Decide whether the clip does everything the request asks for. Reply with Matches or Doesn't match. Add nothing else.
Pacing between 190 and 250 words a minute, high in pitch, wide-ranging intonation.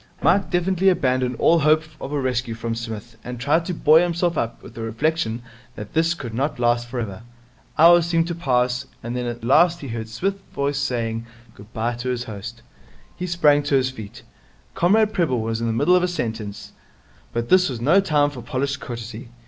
Doesn't match